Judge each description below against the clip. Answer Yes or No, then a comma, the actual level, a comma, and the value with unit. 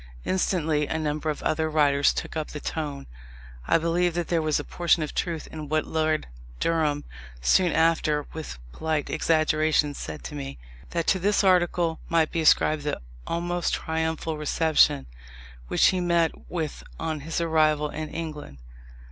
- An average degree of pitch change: No, narrow, 1.8 semitones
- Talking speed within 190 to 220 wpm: No, average, 155 wpm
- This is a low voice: No, medium, 155 Hz